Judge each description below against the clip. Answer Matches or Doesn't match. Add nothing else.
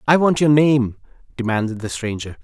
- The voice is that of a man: Matches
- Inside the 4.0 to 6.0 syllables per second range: Matches